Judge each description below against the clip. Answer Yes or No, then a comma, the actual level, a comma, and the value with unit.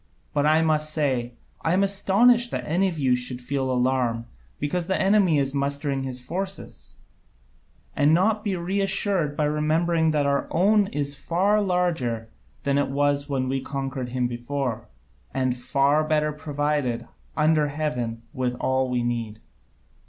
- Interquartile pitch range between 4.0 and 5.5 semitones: Yes, average, 4.7 semitones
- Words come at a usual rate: Yes, average, 150 wpm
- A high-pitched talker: No, medium, 145 Hz